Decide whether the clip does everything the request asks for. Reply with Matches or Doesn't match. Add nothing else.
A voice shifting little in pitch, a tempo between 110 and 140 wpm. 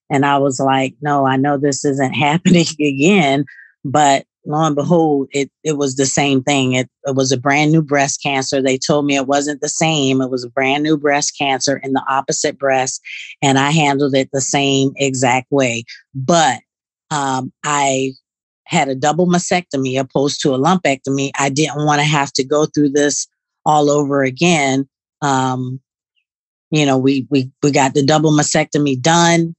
Doesn't match